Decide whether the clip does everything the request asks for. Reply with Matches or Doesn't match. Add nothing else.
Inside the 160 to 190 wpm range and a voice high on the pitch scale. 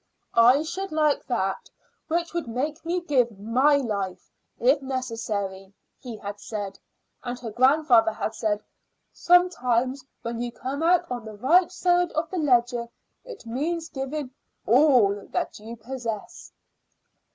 Doesn't match